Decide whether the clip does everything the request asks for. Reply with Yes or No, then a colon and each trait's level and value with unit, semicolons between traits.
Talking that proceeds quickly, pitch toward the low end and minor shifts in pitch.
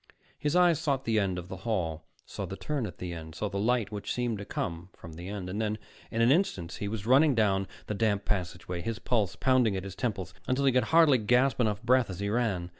No: fast, 245 wpm; low, 105 Hz; average, 4.8 semitones